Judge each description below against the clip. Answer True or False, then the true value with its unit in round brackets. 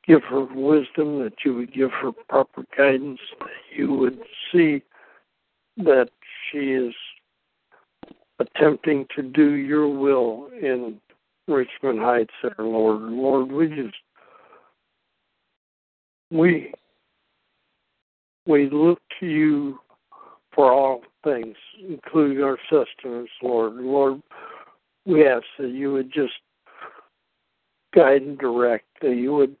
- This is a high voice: False (140 Hz)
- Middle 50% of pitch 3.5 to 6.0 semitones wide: False (2.9 semitones)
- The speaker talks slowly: True (115 wpm)